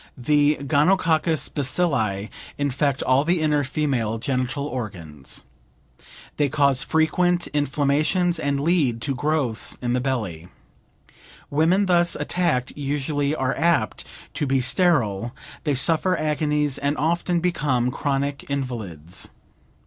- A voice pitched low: No, medium, 145 Hz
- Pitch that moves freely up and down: No, average, 3.8 semitones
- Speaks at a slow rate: Yes, slow, 115 wpm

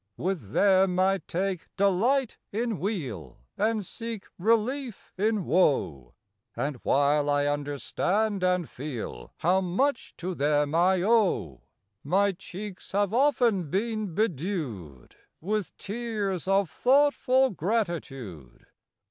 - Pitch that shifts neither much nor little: No, wide, 6.5 semitones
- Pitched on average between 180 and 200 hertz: Yes, high, 190 Hz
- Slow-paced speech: Yes, slow, 110 wpm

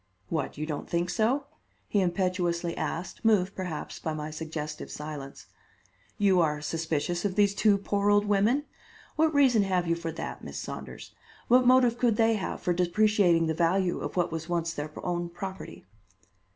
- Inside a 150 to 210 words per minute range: Yes, average, 170 wpm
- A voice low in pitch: No, medium, 180 Hz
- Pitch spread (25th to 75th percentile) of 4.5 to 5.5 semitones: No, average, 3.8 semitones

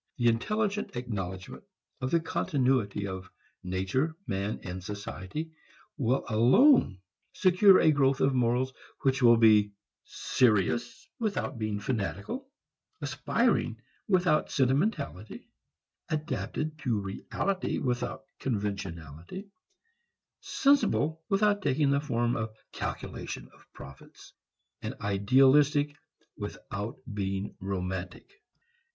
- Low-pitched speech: Yes, low, 125 Hz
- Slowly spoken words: Yes, slow, 95 wpm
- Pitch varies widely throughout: Yes, wide, 7.3 semitones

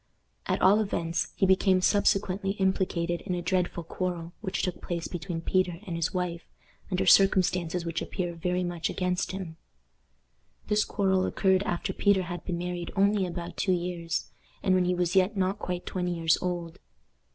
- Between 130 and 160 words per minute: No, average, 170 wpm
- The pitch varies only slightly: Yes, narrow, 1.6 semitones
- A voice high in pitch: No, medium, 180 Hz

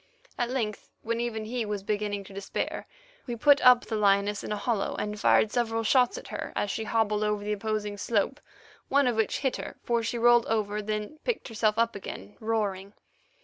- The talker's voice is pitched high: Yes, high, 215 Hz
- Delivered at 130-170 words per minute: No, average, 200 wpm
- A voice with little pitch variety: Yes, narrow, 2.3 semitones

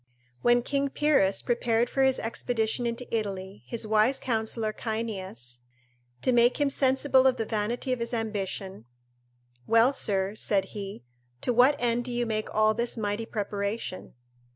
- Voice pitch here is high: Yes, high, 225 Hz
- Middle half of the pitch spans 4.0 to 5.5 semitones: No, average, 2.9 semitones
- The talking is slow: No, average, 155 wpm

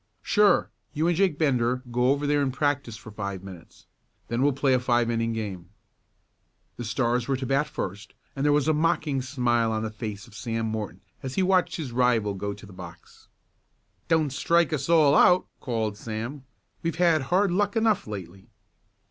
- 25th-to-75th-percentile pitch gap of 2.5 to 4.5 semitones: No, average, 5.3 semitones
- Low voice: Yes, low, 125 Hz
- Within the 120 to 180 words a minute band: No, average, 190 wpm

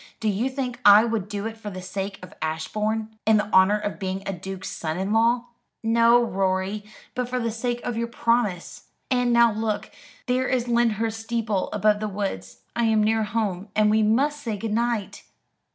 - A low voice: No, high, 220 Hz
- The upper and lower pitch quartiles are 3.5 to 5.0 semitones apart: No, average, 2.7 semitones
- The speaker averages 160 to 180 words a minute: No, average, 195 wpm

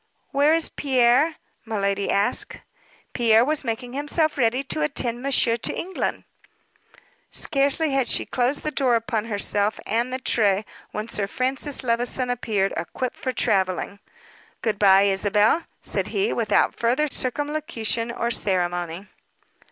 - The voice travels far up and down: No, average, 4.7 semitones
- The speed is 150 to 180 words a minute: No, slow, 135 wpm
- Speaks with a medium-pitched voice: No, high, 235 Hz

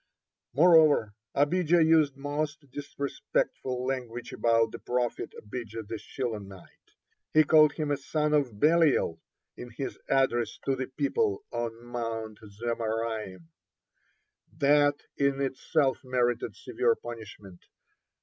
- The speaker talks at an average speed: No, slow, 110 wpm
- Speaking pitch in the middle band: No, low, 130 Hz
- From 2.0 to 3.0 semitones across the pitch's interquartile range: No, average, 4.2 semitones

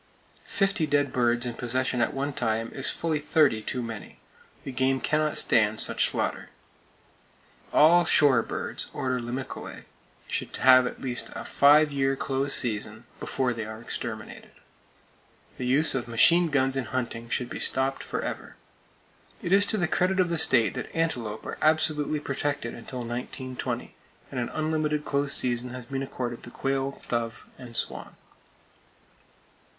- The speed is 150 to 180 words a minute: Yes, average, 155 wpm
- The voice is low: Yes, low, 130 Hz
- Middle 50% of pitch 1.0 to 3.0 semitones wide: No, average, 3.6 semitones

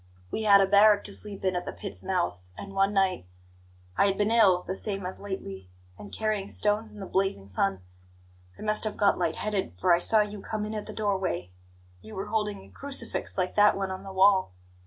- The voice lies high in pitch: Yes, high, 200 Hz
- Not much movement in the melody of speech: Yes, narrow, 2.0 semitones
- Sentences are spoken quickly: Yes, fast, 225 wpm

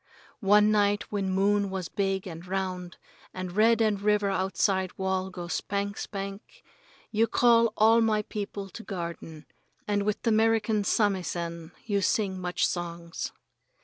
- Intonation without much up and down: Yes, narrow, 2.3 semitones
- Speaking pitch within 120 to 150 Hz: No, high, 200 Hz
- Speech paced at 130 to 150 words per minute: Yes, average, 145 wpm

